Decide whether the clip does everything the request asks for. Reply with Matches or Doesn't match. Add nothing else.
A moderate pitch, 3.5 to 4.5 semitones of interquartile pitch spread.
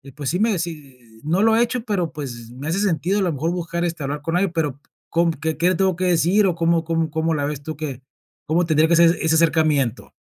Doesn't match